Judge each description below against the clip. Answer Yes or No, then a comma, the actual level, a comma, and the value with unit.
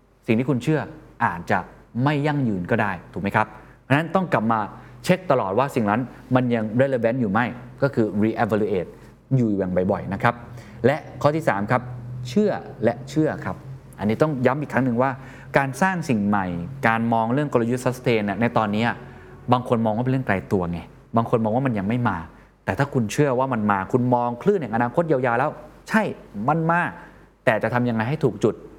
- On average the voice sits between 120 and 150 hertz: Yes, low, 125 Hz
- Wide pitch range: No, average, 3.5 semitones